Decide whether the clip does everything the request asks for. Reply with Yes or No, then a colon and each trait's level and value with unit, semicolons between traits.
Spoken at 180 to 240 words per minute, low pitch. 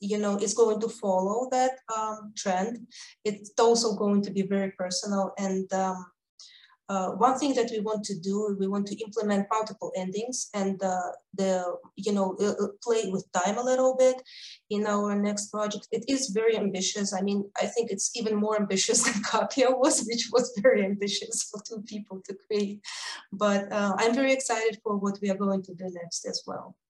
No: average, 190 wpm; high, 210 Hz